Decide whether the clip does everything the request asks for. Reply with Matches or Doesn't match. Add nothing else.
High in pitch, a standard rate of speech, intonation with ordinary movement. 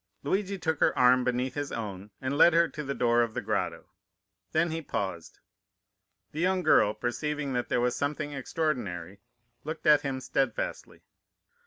Doesn't match